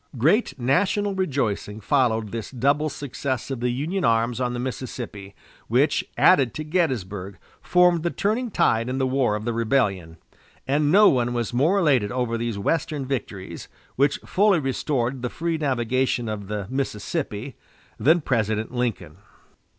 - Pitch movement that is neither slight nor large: Yes, average, 4.7 semitones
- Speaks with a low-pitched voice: Yes, low, 130 Hz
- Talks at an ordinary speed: Yes, average, 150 wpm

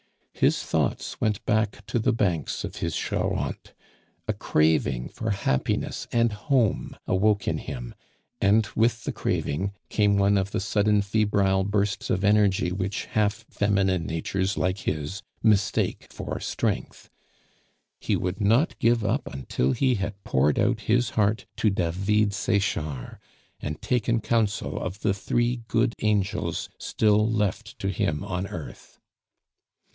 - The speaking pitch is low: Yes, low, 100 Hz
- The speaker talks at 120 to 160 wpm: Yes, average, 140 wpm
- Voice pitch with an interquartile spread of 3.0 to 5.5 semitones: No, narrow, 2.5 semitones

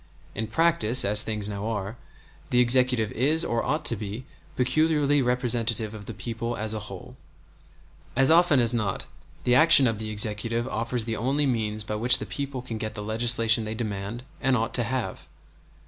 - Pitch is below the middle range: Yes, low, 115 Hz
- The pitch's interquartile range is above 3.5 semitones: No, average, 2.9 semitones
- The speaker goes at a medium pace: Yes, average, 180 wpm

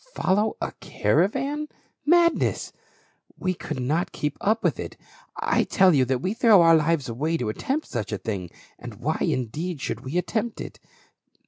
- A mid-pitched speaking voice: Yes, medium, 165 Hz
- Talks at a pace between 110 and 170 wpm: Yes, average, 165 wpm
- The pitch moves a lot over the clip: Yes, wide, 8.8 semitones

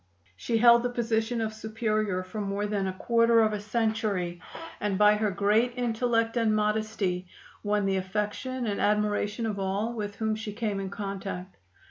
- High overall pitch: Yes, high, 210 Hz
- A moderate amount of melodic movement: No, narrow, 2.0 semitones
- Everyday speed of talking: Yes, average, 170 wpm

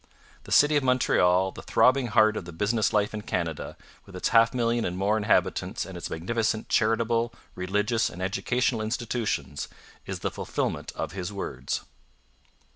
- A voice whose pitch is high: No, low, 110 Hz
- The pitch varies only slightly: No, average, 3.9 semitones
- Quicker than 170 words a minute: No, average, 160 wpm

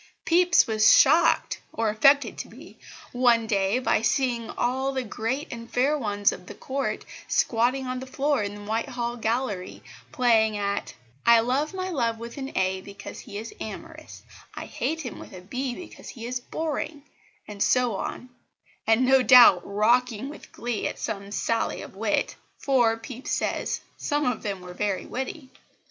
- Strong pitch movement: No, average, 3.7 semitones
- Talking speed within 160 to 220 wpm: Yes, average, 170 wpm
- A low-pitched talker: No, high, 235 Hz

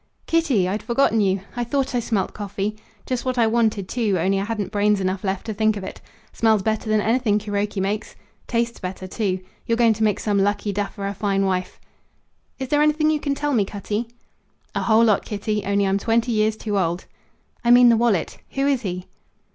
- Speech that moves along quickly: Yes, fast, 210 wpm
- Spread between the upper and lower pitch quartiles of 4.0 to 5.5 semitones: No, average, 3.0 semitones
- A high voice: Yes, high, 215 Hz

